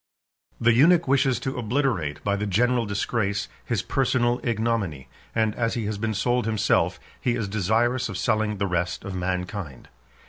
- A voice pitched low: Yes, low, 110 Hz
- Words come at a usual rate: Yes, average, 165 wpm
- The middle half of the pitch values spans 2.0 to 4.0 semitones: Yes, average, 3.7 semitones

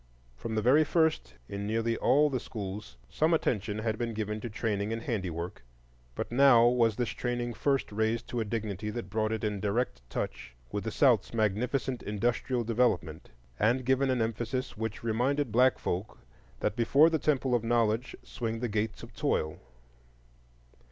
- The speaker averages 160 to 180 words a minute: Yes, average, 170 wpm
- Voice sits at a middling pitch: No, low, 115 Hz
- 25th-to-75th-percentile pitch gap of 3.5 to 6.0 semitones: No, average, 2.9 semitones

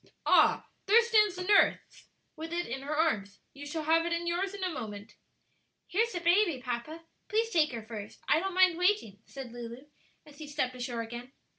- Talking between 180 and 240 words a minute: Yes, average, 195 wpm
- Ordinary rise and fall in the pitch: No, wide, 6.9 semitones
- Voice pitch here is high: Yes, very high, 315 Hz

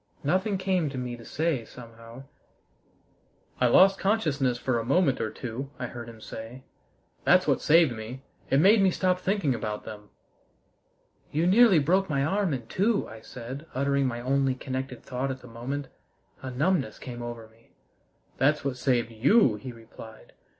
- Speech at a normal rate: Yes, average, 170 wpm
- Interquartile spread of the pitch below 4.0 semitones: No, wide, 5.6 semitones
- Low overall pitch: Yes, low, 130 Hz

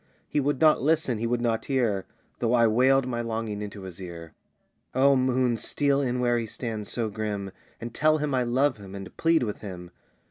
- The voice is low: Yes, low, 120 Hz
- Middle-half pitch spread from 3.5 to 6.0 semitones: Yes, average, 4.0 semitones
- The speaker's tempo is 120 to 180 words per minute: No, fast, 205 wpm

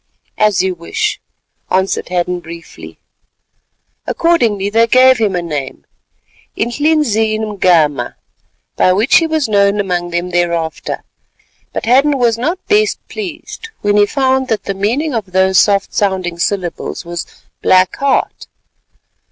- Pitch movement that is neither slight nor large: No, wide, 6.1 semitones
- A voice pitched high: Yes, high, 205 Hz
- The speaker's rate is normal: No, slow, 130 wpm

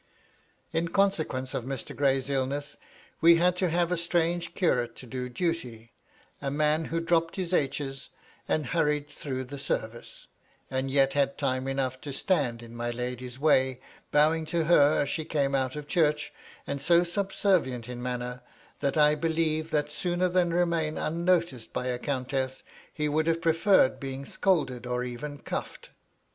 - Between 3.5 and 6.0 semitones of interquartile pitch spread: Yes, average, 4.2 semitones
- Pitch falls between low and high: Yes, medium, 145 Hz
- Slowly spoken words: No, average, 165 wpm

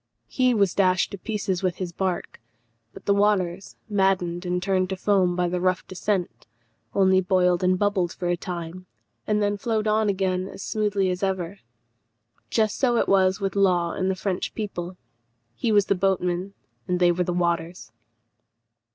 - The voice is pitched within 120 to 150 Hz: No, medium, 185 Hz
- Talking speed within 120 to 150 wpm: No, average, 175 wpm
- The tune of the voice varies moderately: No, narrow, 2.0 semitones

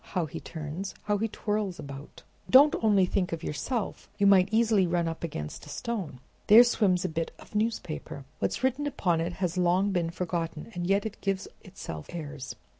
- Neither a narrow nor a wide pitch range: Yes, average, 4.2 semitones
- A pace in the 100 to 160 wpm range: No, average, 190 wpm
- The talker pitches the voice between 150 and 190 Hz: Yes, medium, 185 Hz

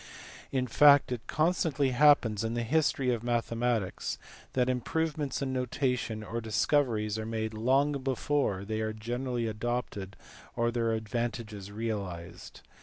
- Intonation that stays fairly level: No, average, 3.3 semitones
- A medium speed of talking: No, slow, 130 wpm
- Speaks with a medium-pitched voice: No, low, 120 Hz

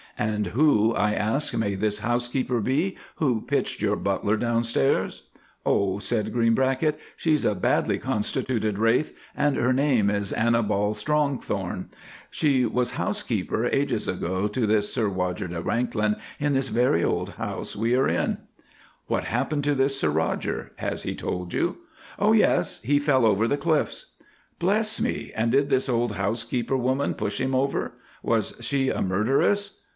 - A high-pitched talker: No, low, 120 Hz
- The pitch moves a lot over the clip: No, average, 4.5 semitones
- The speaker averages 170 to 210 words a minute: No, average, 160 wpm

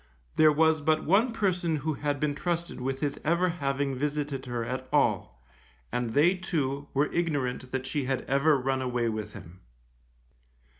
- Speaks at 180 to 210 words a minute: No, average, 165 wpm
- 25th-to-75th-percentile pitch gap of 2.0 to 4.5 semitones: Yes, average, 3.5 semitones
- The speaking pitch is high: No, medium, 145 Hz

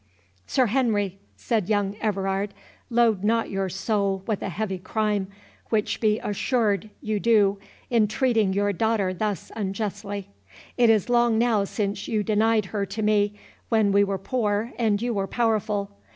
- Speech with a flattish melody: Yes, narrow, 2.1 semitones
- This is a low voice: No, high, 210 Hz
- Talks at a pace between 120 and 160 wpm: Yes, average, 155 wpm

